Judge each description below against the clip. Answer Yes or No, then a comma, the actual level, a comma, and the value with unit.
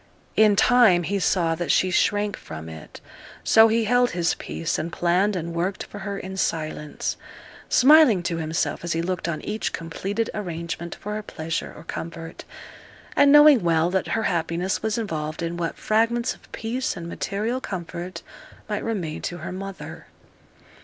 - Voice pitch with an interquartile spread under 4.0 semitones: No, average, 4.4 semitones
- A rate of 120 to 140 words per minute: No, average, 165 wpm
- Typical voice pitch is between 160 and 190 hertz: Yes, medium, 185 Hz